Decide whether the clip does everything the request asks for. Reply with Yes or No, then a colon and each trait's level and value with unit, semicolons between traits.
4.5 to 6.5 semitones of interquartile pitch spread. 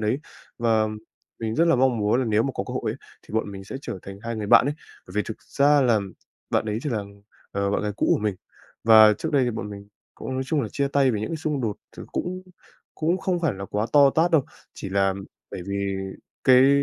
Yes: average, 5.2 semitones